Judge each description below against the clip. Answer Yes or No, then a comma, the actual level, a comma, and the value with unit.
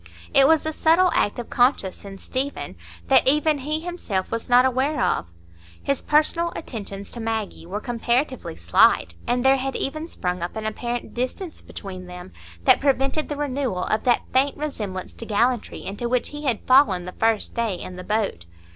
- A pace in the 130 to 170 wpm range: No, average, 180 wpm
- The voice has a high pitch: Yes, high, 245 Hz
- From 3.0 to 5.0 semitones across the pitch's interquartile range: No, wide, 5.6 semitones